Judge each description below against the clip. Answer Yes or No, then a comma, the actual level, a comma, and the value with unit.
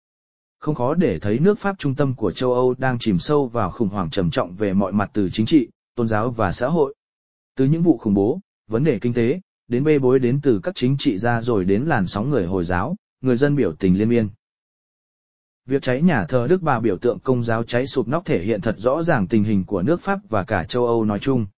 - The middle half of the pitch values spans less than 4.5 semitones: No, average, 4.9 semitones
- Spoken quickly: Yes, fast, 250 wpm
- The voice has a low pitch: Yes, low, 125 Hz